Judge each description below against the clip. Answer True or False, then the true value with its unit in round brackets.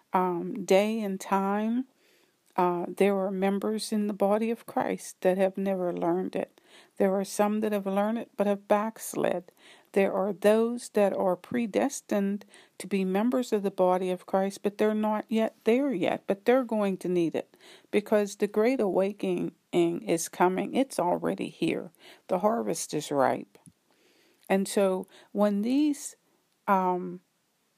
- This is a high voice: True (200 Hz)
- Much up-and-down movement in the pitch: False (2.7 semitones)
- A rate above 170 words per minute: False (155 wpm)